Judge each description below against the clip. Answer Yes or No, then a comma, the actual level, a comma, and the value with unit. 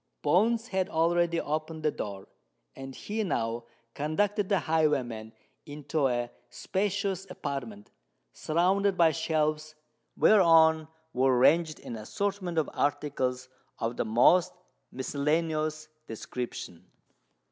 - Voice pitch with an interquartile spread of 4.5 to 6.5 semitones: Yes, wide, 5.4 semitones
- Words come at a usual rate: No, slow, 105 wpm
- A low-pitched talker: No, medium, 155 Hz